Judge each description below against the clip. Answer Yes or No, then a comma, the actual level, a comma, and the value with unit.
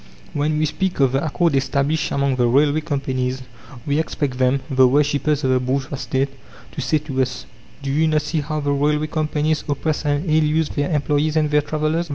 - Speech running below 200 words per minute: No, fast, 205 wpm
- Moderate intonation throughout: No, narrow, 2.1 semitones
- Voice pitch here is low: No, medium, 145 Hz